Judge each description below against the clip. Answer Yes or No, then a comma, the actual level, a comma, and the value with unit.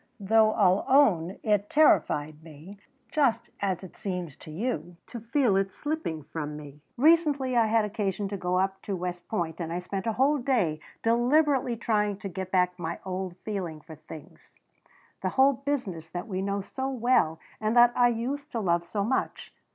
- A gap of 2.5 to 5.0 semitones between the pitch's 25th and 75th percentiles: No, wide, 5.4 semitones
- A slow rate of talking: No, average, 180 wpm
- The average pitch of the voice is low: No, high, 200 Hz